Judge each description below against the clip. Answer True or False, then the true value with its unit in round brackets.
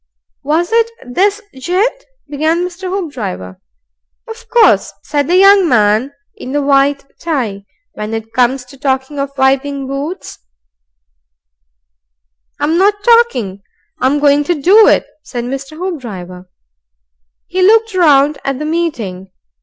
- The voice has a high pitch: True (280 Hz)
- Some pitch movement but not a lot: False (6.8 semitones)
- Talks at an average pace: False (130 wpm)